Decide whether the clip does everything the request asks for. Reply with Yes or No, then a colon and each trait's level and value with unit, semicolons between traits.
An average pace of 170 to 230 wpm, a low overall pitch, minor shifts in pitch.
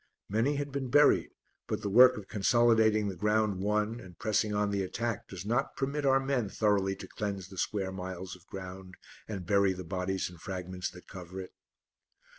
No: average, 190 wpm; low, 100 Hz; average, 3.3 semitones